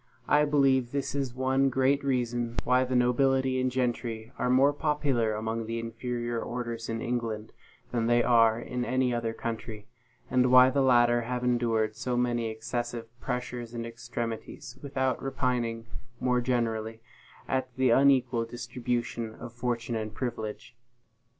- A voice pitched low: Yes, low, 120 Hz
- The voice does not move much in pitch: Yes, narrow, 1.9 semitones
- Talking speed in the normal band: Yes, average, 145 wpm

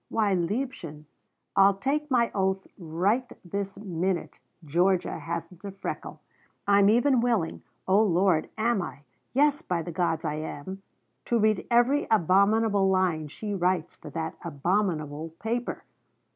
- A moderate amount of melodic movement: Yes, average, 4.5 semitones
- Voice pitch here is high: Yes, high, 195 Hz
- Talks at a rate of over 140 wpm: No, slow, 135 wpm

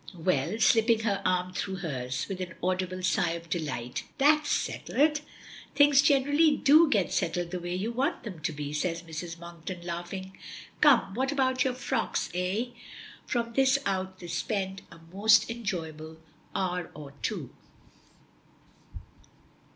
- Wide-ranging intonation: Yes, wide, 5.8 semitones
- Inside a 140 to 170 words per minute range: Yes, average, 145 wpm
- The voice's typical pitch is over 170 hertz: Yes, medium, 185 Hz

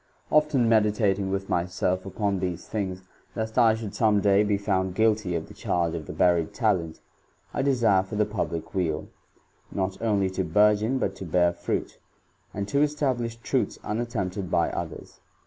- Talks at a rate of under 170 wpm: Yes, average, 160 wpm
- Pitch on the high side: No, low, 100 Hz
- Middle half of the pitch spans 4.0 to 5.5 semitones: No, average, 3.3 semitones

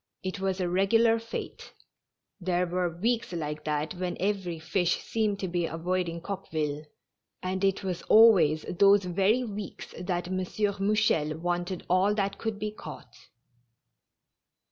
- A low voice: No, medium, 185 Hz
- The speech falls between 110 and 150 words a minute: Yes, average, 145 wpm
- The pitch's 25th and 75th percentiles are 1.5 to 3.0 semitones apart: Yes, average, 2.7 semitones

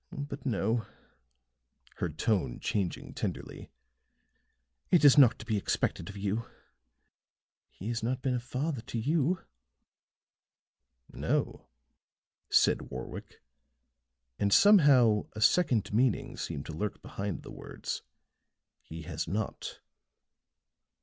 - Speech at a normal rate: No, slow, 110 wpm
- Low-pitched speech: Yes, low, 115 Hz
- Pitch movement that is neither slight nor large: Yes, average, 4.9 semitones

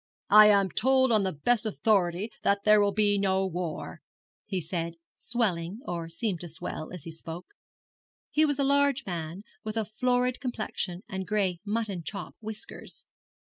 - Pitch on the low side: No, high, 200 Hz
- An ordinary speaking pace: Yes, average, 165 wpm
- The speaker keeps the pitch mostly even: No, average, 4.2 semitones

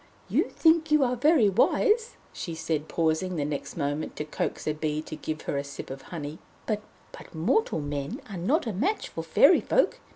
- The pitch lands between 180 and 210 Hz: No, medium, 170 Hz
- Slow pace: No, average, 195 wpm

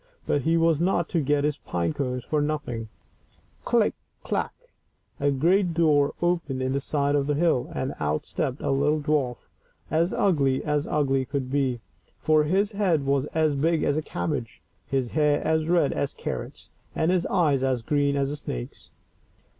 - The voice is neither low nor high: Yes, medium, 145 Hz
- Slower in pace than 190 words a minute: Yes, average, 180 wpm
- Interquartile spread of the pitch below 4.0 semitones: Yes, average, 2.8 semitones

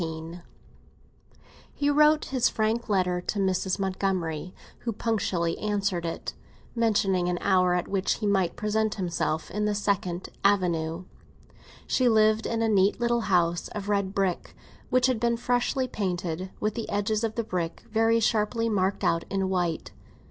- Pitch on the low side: No, high, 200 Hz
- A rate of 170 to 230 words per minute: No, average, 155 wpm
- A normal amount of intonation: Yes, average, 3.7 semitones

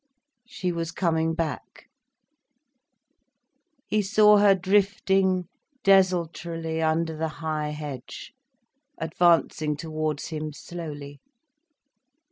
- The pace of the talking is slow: Yes, slow, 85 wpm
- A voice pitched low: No, medium, 165 Hz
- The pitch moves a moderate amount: Yes, average, 3.2 semitones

